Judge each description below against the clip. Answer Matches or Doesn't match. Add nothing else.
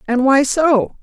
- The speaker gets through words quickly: Doesn't match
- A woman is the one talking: Matches